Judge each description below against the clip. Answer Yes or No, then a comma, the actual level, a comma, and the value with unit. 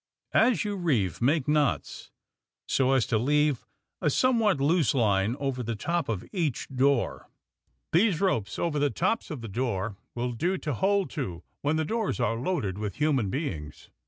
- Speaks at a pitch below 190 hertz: Yes, medium, 140 Hz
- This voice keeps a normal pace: Yes, average, 175 wpm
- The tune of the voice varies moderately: No, wide, 6.7 semitones